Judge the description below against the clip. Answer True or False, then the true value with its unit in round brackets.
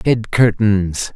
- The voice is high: False (105 Hz)